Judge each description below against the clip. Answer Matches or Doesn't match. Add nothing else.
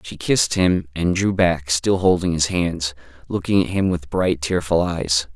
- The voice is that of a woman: Doesn't match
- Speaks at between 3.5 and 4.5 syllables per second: Matches